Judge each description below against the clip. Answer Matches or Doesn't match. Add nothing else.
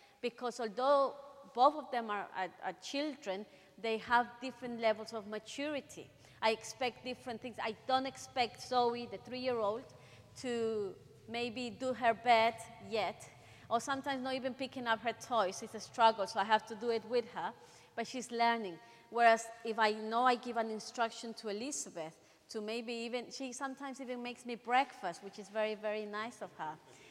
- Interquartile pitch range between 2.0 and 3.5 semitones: Matches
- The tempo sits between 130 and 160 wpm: Doesn't match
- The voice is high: Matches